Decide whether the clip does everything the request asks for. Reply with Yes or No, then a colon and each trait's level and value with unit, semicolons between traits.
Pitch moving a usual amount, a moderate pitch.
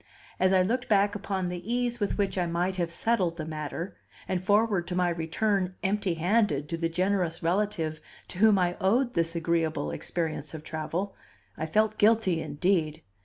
Yes: average, 3.7 semitones; medium, 180 Hz